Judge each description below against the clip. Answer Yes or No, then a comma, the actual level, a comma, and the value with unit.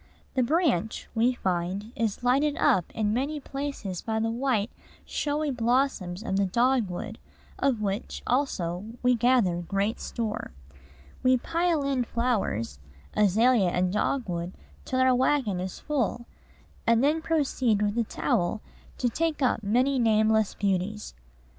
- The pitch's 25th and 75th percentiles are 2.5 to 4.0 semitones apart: No, average, 4.7 semitones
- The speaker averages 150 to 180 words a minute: No, slow, 135 wpm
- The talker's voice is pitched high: Yes, high, 230 Hz